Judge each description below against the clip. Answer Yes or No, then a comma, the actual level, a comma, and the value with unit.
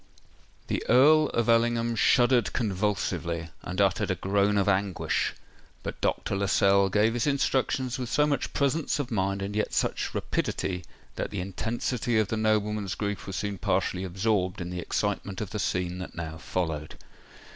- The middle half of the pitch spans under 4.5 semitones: Yes, average, 3.8 semitones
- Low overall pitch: Yes, low, 105 Hz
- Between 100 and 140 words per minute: No, average, 165 wpm